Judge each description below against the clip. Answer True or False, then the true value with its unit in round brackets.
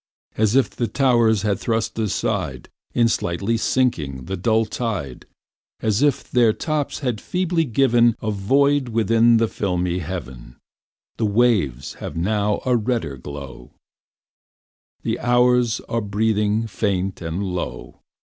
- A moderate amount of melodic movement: True (4.3 semitones)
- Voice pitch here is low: True (110 Hz)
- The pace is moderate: False (130 wpm)